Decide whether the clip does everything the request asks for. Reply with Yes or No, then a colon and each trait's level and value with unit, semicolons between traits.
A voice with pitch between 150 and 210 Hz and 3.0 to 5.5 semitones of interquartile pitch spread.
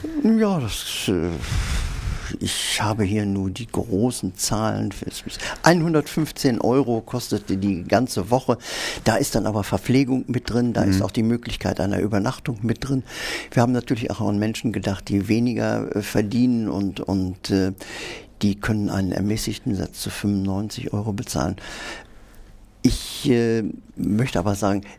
No: low, 105 Hz; average, 3.6 semitones